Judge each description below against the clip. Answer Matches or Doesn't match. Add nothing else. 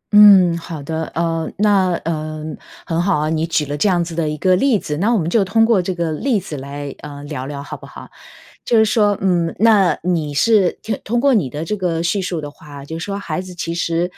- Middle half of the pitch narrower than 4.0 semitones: Doesn't match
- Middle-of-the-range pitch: Matches